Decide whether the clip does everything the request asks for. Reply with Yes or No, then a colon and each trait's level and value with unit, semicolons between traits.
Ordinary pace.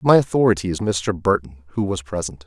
Yes: average, 195 wpm